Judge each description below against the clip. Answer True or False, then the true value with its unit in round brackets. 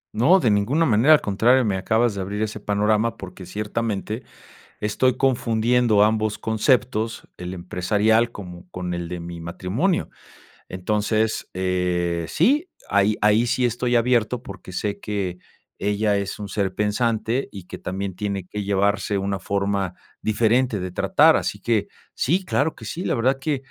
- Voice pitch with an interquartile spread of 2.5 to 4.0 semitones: True (3.4 semitones)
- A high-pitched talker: False (105 Hz)